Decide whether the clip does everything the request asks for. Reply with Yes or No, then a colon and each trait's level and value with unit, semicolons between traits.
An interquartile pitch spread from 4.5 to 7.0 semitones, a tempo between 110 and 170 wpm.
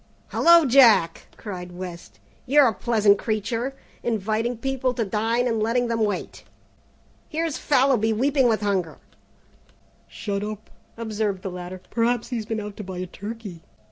No: average, 3.3 semitones; average, 150 wpm